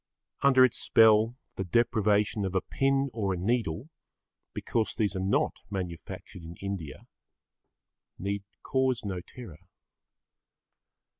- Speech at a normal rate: No, slow, 120 wpm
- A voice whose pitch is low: Yes, low, 100 Hz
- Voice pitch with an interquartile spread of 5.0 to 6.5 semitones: No, average, 4.1 semitones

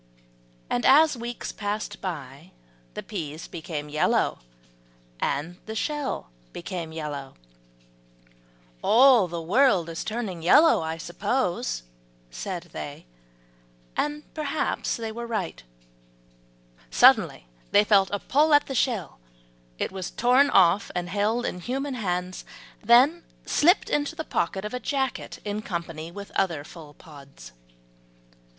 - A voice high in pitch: Yes, high, 195 Hz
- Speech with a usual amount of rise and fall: No, wide, 7.2 semitones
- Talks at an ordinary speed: No, slow, 125 wpm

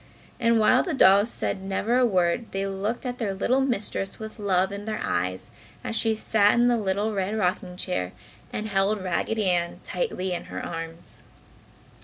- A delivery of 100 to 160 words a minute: No, average, 180 wpm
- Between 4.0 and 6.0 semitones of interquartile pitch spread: No, average, 3.1 semitones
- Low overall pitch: No, high, 200 Hz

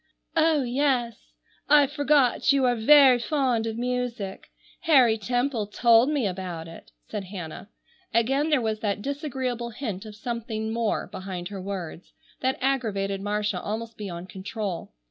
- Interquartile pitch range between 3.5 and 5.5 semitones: Yes, average, 4.6 semitones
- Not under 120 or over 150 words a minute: Yes, average, 145 wpm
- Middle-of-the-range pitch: No, high, 230 Hz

